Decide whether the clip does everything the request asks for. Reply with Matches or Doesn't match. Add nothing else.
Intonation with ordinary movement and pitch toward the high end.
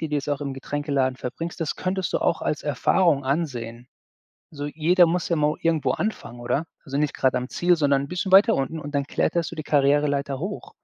Doesn't match